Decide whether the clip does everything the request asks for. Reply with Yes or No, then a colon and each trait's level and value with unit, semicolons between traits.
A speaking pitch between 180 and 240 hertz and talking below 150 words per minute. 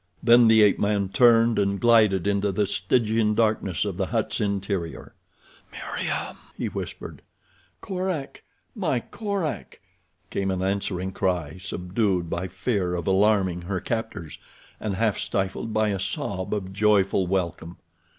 No: low, 100 Hz; slow, 135 wpm